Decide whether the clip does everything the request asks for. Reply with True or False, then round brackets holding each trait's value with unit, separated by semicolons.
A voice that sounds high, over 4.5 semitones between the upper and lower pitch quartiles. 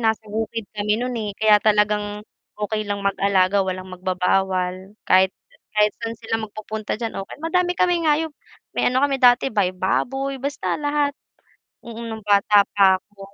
False (210 Hz; 3.5 semitones)